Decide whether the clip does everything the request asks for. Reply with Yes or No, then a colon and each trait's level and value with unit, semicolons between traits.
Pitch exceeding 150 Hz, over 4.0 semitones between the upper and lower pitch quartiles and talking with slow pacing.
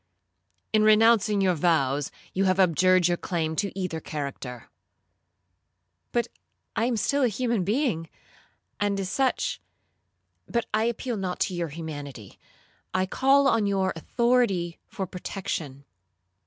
Yes: medium, 185 Hz; wide, 5.4 semitones; slow, 125 wpm